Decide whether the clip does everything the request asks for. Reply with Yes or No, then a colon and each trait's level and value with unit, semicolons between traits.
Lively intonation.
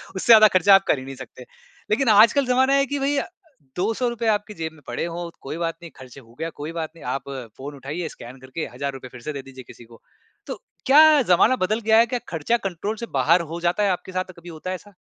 Yes: wide, 7.7 semitones